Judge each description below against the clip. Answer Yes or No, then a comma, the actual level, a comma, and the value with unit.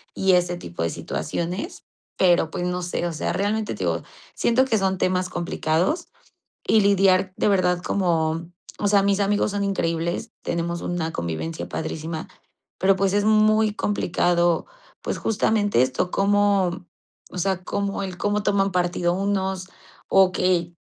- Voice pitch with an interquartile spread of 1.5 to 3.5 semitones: Yes, narrow, 2.6 semitones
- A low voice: No, medium, 185 Hz